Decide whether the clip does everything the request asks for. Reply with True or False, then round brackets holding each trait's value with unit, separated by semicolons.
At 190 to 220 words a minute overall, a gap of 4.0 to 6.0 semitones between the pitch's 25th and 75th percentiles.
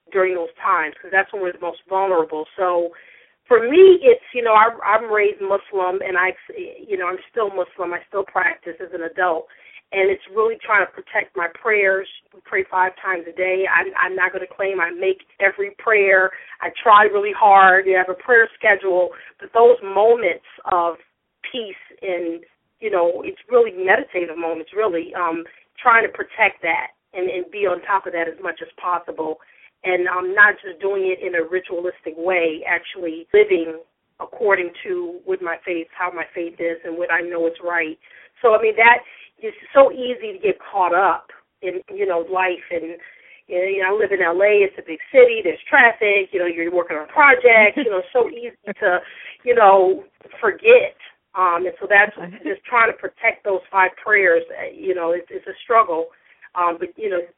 True (195 wpm; 4.4 semitones)